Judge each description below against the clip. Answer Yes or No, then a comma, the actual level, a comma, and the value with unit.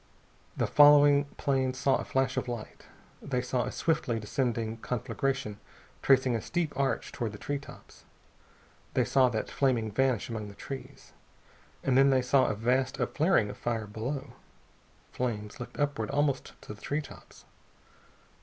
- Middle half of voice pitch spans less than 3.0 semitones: No, average, 3.3 semitones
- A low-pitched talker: Yes, low, 130 Hz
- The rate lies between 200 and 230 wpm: No, average, 155 wpm